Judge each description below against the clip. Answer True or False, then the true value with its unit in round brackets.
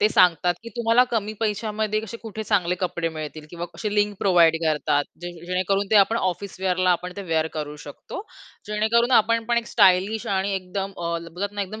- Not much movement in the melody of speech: False (3.5 semitones)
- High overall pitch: True (195 Hz)